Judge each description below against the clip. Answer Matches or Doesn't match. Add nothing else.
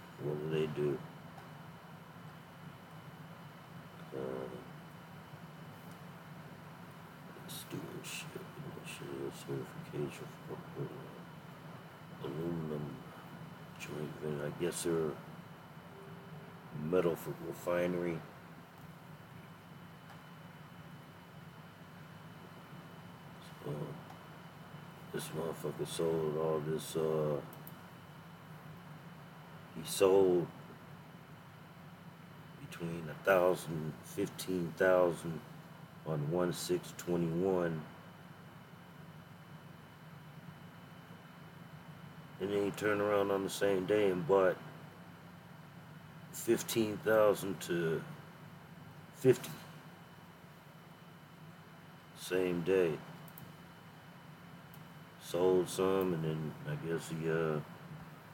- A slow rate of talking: Matches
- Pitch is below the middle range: Doesn't match